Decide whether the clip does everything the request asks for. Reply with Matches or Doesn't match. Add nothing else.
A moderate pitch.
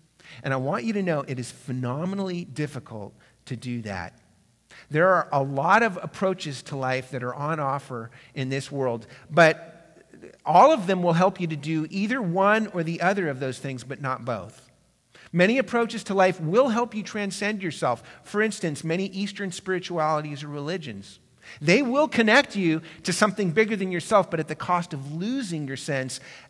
Matches